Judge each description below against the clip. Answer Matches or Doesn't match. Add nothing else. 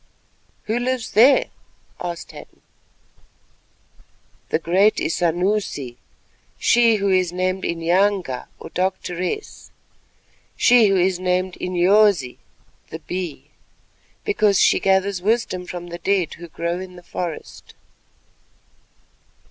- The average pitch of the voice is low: Doesn't match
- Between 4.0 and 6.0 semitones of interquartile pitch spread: Doesn't match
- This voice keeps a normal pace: Doesn't match